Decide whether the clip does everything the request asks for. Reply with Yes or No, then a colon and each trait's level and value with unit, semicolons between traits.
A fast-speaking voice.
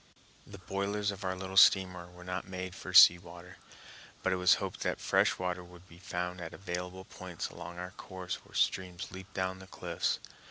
No: average, 195 wpm